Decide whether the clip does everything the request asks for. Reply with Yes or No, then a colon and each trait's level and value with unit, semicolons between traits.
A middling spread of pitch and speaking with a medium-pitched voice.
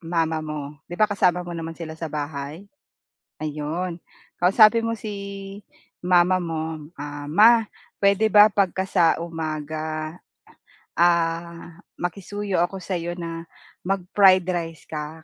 Yes: average, 3.4 semitones; medium, 170 Hz